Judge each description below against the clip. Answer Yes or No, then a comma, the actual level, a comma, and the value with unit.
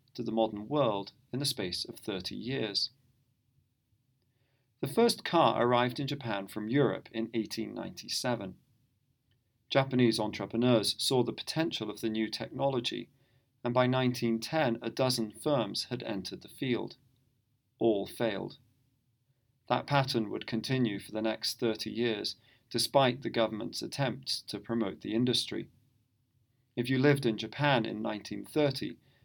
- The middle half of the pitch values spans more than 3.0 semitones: No, narrow, 2.6 semitones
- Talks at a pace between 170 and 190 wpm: No, slow, 135 wpm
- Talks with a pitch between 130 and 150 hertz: No, low, 120 Hz